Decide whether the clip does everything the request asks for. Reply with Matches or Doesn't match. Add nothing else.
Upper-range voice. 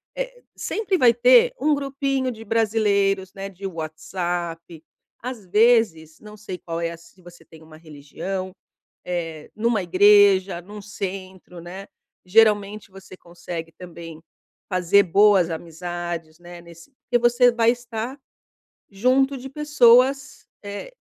Matches